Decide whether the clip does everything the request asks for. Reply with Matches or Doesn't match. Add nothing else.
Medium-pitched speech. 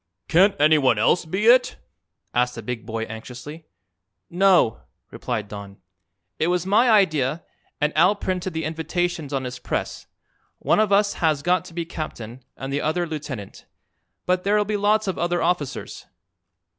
Matches